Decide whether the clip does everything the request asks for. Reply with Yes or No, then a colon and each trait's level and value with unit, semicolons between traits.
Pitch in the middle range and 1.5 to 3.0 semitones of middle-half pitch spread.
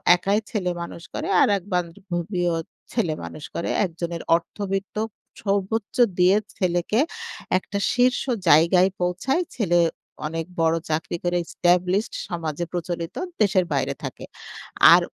Yes: medium, 180 Hz; narrow, 2.5 semitones